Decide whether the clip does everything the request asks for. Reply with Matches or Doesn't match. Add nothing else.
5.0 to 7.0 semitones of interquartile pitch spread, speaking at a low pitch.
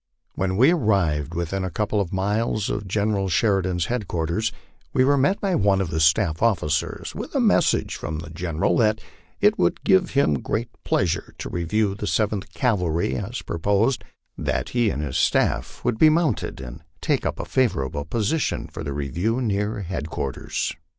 Matches